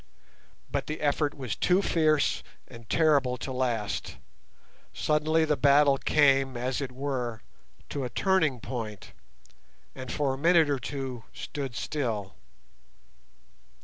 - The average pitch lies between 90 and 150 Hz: Yes, low, 135 Hz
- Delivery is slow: Yes, slow, 125 wpm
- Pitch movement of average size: Yes, average, 3.3 semitones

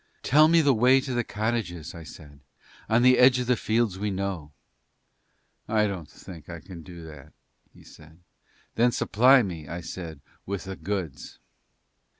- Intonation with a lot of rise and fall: Yes, wide, 6.4 semitones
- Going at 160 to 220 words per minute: Yes, average, 165 wpm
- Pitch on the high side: No, low, 100 Hz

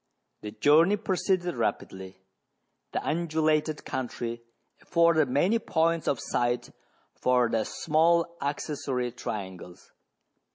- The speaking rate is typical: No, slow, 100 wpm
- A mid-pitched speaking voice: Yes, medium, 150 Hz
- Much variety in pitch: Yes, wide, 5.7 semitones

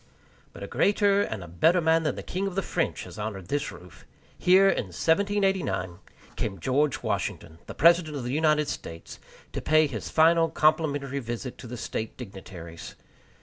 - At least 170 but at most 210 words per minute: Yes, average, 175 wpm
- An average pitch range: No, wide, 7.6 semitones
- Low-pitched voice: No, medium, 145 Hz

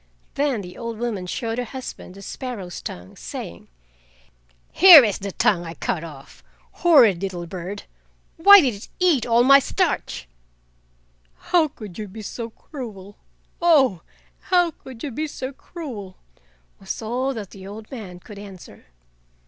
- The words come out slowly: No, average, 150 wpm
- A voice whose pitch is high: Yes, high, 225 Hz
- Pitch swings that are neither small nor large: No, wide, 6.0 semitones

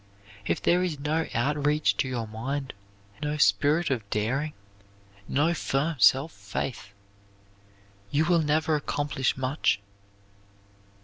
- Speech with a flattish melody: No, average, 3.2 semitones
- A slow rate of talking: Yes, slow, 120 wpm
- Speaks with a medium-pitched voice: Yes, medium, 145 Hz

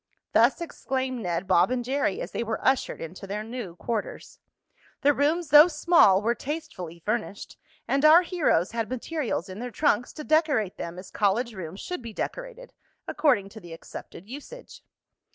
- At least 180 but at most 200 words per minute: No, average, 170 wpm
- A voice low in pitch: No, high, 240 Hz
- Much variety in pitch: Yes, wide, 7.2 semitones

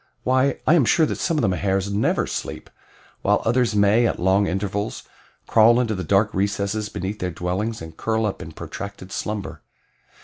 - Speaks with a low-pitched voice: Yes, low, 105 Hz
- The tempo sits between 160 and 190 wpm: Yes, average, 180 wpm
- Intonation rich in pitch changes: No, average, 2.8 semitones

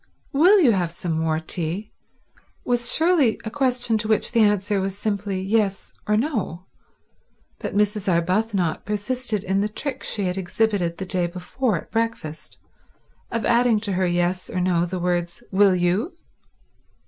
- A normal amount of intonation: Yes, average, 3.9 semitones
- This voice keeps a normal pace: Yes, average, 160 wpm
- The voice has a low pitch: No, high, 200 Hz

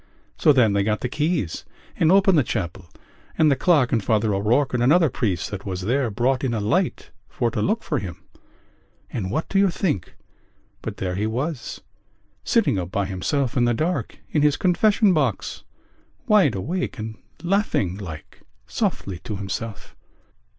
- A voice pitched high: No, low, 120 Hz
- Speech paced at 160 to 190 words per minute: Yes, average, 170 wpm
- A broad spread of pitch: Yes, wide, 7.8 semitones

